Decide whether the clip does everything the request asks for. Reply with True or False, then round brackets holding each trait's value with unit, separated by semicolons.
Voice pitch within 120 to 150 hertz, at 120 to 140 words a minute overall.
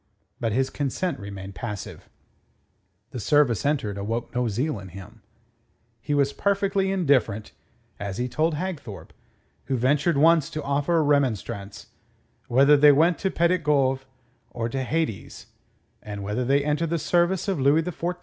False (140 Hz; 160 wpm)